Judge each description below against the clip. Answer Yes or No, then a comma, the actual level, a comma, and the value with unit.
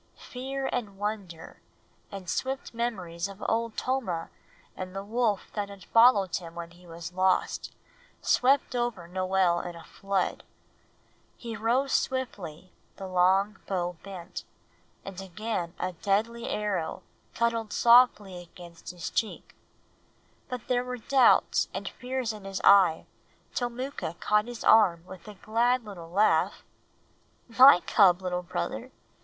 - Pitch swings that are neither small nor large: Yes, average, 4.7 semitones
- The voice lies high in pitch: Yes, high, 200 Hz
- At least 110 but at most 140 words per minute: Yes, slow, 135 wpm